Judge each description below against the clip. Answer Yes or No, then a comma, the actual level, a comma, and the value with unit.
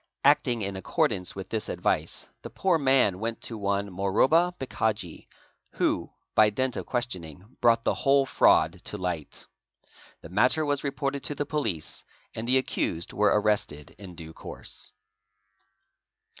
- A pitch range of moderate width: No, wide, 6.0 semitones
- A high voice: No, low, 110 Hz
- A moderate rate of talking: Yes, average, 145 wpm